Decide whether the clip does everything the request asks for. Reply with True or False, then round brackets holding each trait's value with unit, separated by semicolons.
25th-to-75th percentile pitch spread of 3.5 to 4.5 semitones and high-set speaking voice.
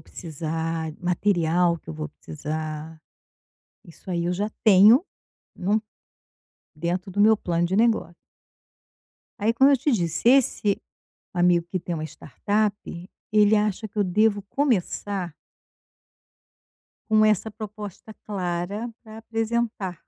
True (4.1 semitones; 195 Hz)